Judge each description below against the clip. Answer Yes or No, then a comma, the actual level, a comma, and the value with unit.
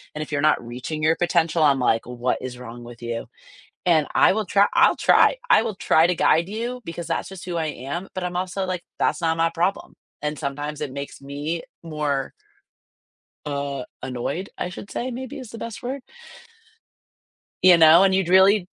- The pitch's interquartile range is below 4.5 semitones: No, average, 5.0 semitones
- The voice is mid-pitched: Yes, medium, 165 Hz